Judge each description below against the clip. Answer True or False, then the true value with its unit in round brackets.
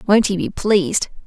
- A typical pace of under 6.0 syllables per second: True (5.2 syllables/s)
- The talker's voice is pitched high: True (195 Hz)